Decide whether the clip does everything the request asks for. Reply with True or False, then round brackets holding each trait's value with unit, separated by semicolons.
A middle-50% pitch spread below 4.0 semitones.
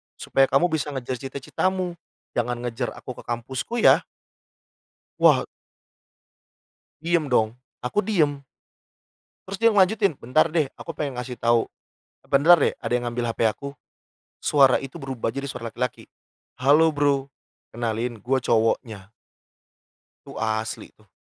False (4.4 semitones)